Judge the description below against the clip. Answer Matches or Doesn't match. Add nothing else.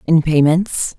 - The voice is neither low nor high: Matches